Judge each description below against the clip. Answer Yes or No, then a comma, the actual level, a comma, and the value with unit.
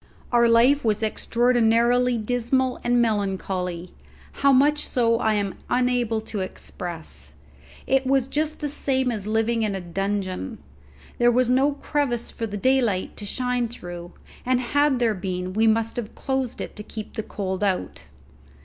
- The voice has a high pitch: Yes, high, 230 Hz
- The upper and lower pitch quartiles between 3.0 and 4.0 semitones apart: Yes, average, 3.5 semitones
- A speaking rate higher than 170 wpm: No, average, 160 wpm